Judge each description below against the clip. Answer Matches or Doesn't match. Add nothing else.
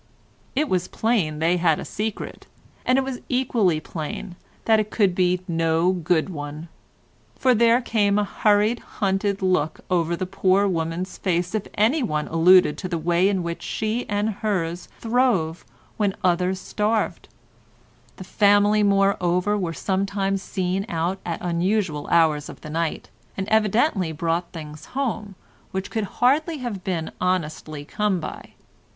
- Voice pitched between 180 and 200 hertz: Matches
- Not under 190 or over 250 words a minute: Doesn't match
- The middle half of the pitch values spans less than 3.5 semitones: Doesn't match